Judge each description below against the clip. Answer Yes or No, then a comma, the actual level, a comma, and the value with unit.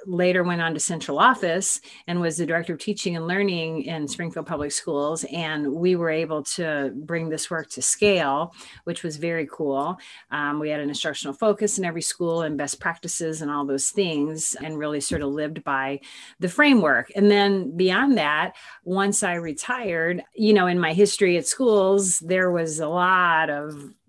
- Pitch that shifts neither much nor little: Yes, average, 3.4 semitones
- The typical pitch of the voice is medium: Yes, medium, 165 Hz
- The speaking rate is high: No, average, 185 wpm